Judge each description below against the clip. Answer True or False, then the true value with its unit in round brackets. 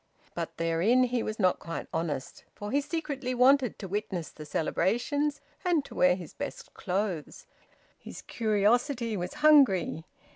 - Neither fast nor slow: True (145 wpm)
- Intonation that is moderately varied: False (7.1 semitones)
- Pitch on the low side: False (215 Hz)